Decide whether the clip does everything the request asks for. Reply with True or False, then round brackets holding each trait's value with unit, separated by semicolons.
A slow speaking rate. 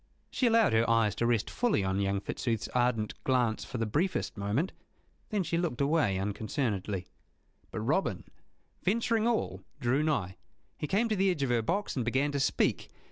False (180 wpm)